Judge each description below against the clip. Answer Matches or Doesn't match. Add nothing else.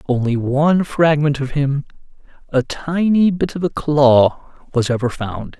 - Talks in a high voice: Doesn't match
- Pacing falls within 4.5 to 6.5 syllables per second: Doesn't match